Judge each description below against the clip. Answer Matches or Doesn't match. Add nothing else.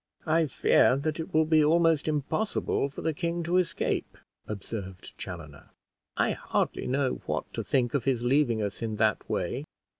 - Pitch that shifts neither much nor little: Doesn't match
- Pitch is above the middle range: Doesn't match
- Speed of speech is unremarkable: Matches